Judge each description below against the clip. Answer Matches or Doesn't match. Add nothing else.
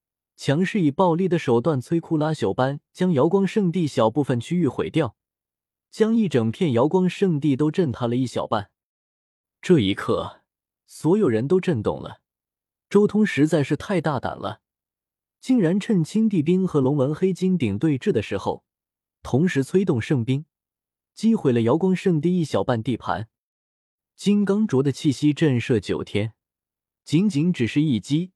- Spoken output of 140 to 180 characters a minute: Doesn't match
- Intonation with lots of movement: Matches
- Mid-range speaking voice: Matches